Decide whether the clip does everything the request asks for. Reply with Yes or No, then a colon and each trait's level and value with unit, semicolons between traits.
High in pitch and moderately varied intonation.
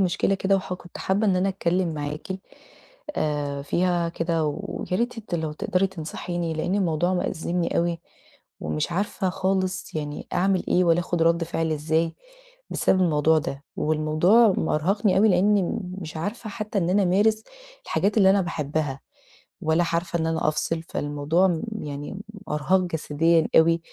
No: medium, 170 Hz; average, 3.2 semitones